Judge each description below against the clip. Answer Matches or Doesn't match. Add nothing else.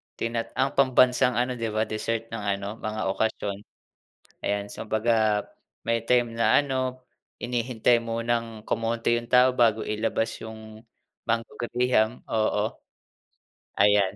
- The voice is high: Doesn't match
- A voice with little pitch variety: Matches